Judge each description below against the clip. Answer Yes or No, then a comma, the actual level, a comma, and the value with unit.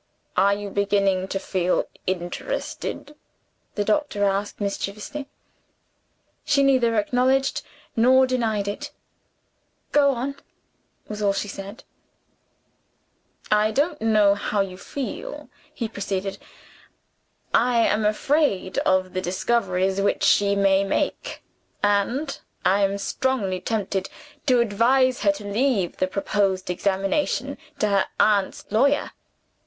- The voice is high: Yes, high, 205 Hz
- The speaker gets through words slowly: Yes, slow, 115 wpm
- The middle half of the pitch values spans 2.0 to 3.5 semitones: No, average, 4.3 semitones